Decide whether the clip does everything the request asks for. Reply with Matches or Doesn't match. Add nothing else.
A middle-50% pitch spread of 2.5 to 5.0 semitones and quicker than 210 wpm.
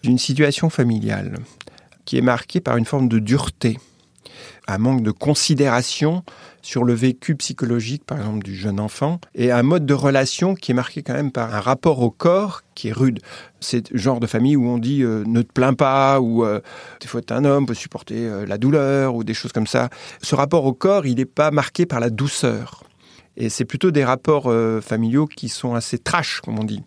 Matches